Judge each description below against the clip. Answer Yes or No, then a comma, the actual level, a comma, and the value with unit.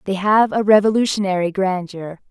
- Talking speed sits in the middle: No, slow, 130 wpm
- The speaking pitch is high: Yes, high, 195 Hz